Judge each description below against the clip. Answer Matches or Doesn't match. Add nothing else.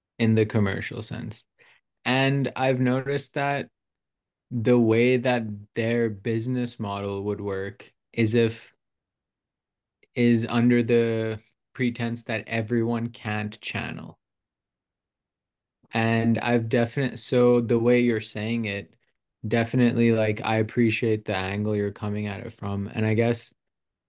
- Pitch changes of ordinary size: Doesn't match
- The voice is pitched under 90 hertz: Doesn't match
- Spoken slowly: Matches